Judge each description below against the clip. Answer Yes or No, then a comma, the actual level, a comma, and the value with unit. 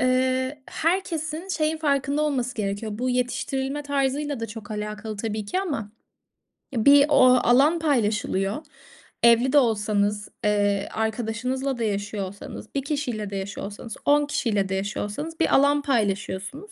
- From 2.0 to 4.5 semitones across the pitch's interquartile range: No, wide, 5.4 semitones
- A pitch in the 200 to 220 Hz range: No, high, 245 Hz